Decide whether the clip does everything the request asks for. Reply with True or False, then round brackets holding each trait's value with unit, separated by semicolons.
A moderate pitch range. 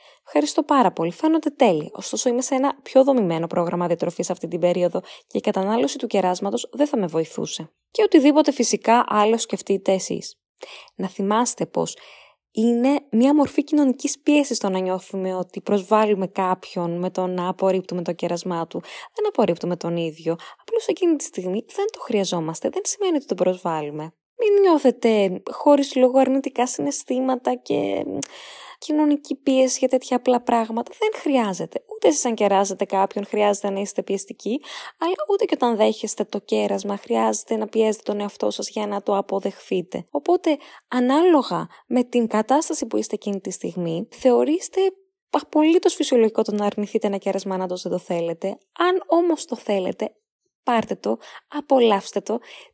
False (7.3 semitones)